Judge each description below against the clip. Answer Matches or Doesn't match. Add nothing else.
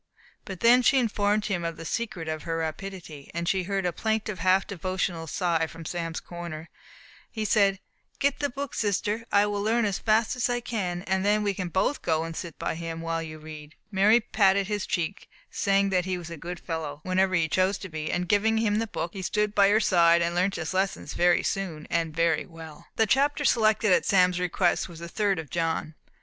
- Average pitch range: Matches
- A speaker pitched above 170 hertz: Matches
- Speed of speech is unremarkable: Doesn't match